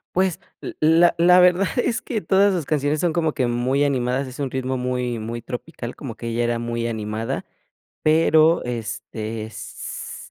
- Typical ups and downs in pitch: No, wide, 5.7 semitones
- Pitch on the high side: No, low, 130 Hz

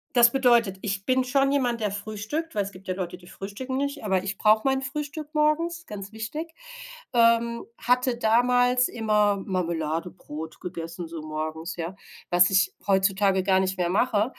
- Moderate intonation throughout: Yes, average, 5.0 semitones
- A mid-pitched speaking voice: No, high, 210 Hz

